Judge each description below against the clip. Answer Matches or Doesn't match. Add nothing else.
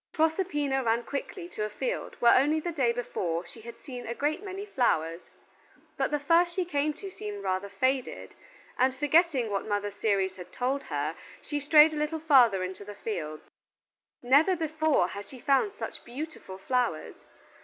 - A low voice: Doesn't match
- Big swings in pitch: Matches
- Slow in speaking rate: Doesn't match